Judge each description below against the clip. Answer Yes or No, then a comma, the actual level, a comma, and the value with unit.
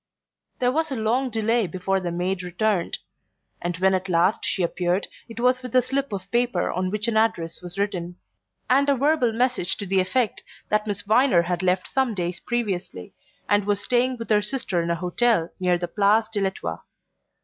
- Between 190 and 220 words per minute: Yes, average, 195 wpm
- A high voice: Yes, high, 205 Hz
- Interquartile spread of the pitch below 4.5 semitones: No, average, 5.0 semitones